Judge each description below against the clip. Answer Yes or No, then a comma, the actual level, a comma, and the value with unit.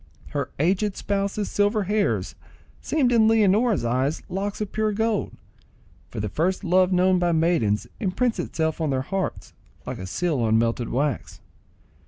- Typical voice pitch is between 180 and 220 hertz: Yes, medium, 185 Hz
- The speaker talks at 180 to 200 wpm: No, average, 155 wpm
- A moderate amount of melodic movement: No, wide, 6.0 semitones